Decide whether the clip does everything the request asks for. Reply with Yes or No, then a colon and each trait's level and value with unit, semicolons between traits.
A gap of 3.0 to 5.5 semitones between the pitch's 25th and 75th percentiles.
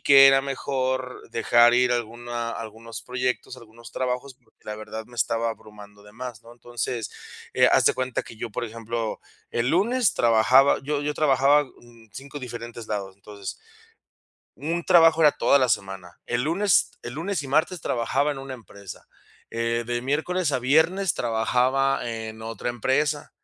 Yes: average, 3.4 semitones